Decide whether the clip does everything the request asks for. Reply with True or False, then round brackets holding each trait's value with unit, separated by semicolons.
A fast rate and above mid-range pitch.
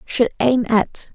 False (155 wpm; 230 Hz)